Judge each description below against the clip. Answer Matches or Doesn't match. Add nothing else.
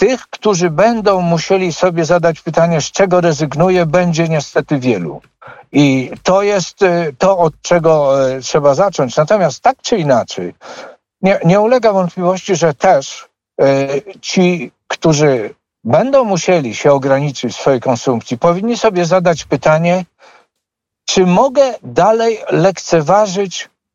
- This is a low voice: Doesn't match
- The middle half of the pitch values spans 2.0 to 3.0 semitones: Doesn't match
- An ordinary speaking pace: Matches